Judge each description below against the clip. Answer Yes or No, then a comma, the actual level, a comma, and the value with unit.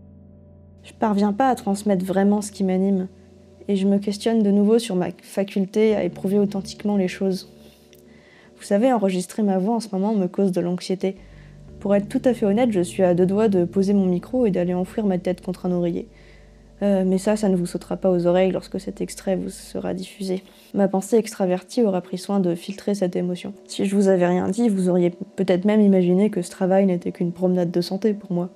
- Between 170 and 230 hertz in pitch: Yes, high, 190 Hz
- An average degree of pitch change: No, narrow, 2.1 semitones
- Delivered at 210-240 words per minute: Yes, fast, 220 wpm